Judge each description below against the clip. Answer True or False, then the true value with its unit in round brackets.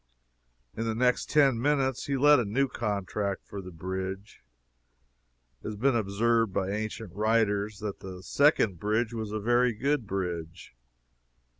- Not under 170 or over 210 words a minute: False (150 wpm)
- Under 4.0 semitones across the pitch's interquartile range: True (3.6 semitones)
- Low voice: True (110 Hz)